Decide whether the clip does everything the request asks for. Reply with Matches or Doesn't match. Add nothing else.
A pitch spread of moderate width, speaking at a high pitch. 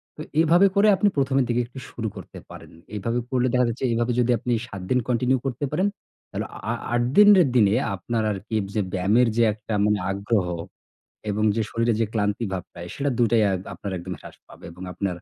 Doesn't match